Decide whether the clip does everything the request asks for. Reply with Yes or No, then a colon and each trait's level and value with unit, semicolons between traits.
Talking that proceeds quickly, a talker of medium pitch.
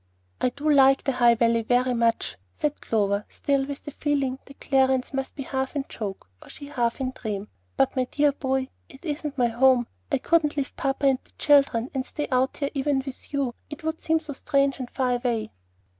No: fast, 210 wpm; very high, 265 Hz